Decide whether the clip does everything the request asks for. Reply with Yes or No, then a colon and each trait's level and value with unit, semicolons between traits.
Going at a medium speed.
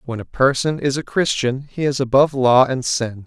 No: fast, 220 wpm